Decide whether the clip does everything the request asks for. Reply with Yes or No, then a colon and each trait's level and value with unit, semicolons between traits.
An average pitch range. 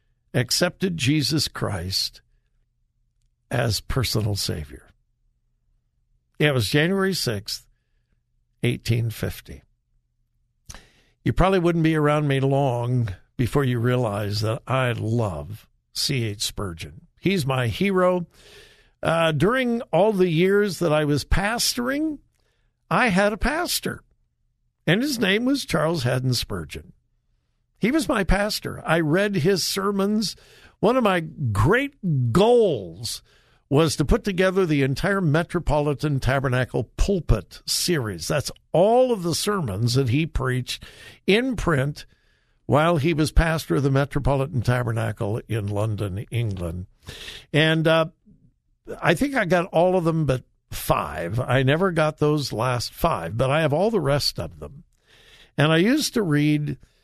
No: wide, 7.4 semitones